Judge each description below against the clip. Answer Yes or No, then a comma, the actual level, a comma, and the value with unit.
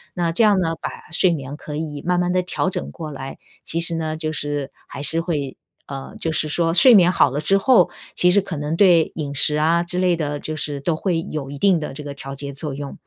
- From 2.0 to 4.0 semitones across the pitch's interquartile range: Yes, average, 3.3 semitones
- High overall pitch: No, medium, 160 Hz